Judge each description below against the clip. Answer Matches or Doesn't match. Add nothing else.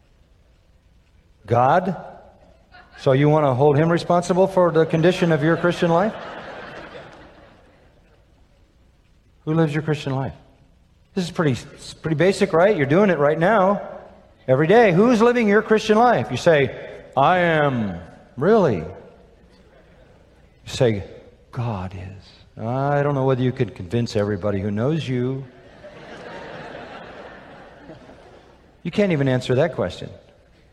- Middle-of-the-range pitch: Matches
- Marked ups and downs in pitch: Matches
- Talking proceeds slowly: Matches